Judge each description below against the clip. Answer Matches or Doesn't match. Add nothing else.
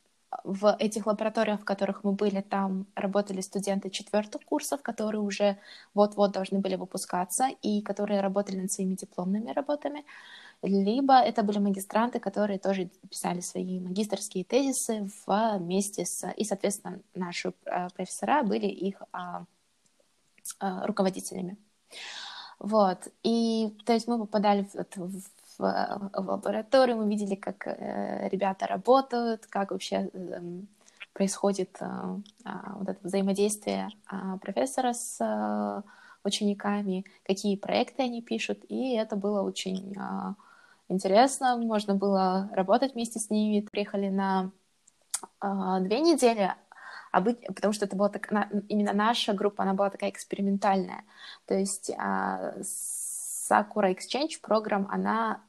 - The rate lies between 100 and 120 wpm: Matches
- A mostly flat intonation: Matches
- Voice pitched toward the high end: Matches